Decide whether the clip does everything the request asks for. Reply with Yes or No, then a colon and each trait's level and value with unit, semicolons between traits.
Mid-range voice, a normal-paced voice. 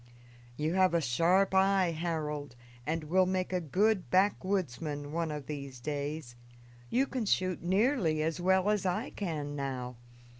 Yes: medium, 170 Hz; average, 150 wpm